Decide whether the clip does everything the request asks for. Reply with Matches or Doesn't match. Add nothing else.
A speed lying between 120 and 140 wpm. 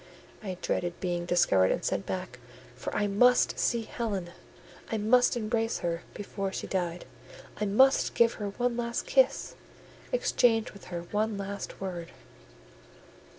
Matches